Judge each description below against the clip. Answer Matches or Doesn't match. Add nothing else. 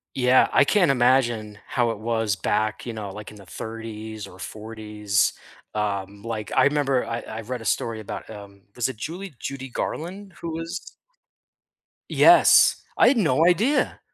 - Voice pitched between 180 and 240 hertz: Doesn't match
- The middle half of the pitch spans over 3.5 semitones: Matches